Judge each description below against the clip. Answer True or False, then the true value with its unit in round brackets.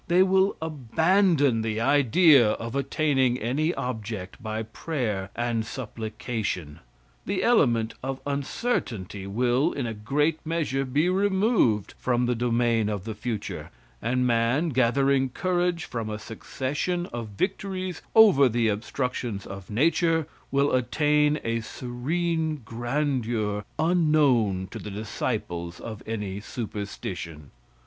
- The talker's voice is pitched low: True (125 Hz)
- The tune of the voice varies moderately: False (5.7 semitones)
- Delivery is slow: True (120 wpm)